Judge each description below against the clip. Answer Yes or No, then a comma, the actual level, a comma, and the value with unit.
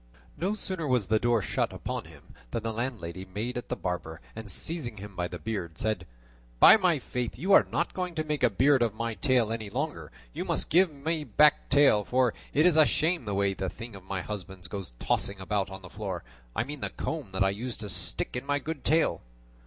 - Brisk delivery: Yes, fast, 230 wpm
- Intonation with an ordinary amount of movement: No, wide, 7.0 semitones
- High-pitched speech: No, low, 115 Hz